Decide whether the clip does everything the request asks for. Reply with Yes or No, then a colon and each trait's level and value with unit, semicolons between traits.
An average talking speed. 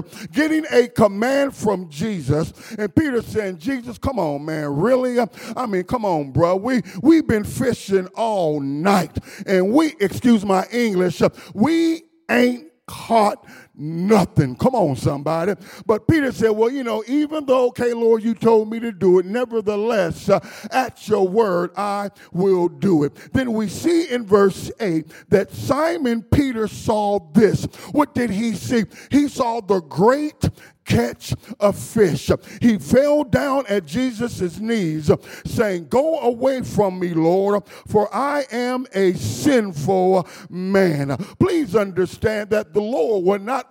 Yes: average, 150 wpm